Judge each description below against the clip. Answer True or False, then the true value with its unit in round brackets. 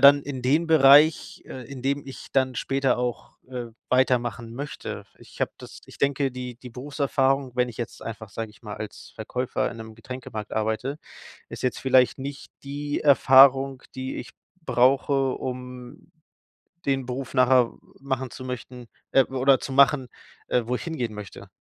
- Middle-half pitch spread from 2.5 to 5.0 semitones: False (1.9 semitones)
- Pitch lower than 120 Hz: False (130 Hz)